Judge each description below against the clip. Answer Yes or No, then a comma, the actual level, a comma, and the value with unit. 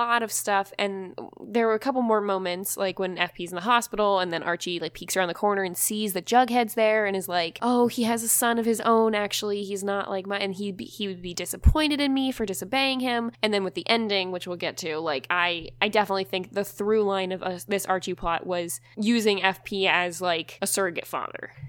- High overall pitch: Yes, high, 200 Hz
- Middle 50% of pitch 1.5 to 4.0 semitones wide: Yes, average, 3.7 semitones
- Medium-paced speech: No, fast, 240 wpm